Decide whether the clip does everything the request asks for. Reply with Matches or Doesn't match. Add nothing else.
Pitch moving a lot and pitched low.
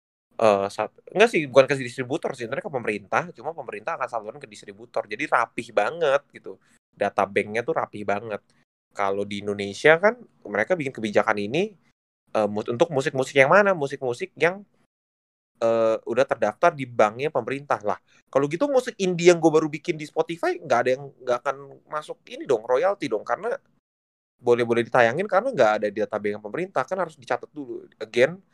Matches